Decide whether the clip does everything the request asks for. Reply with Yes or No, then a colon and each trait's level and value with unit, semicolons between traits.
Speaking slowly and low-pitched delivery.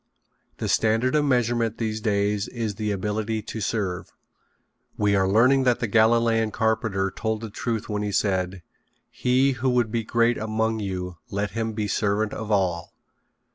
No: average, 165 wpm; low, 110 Hz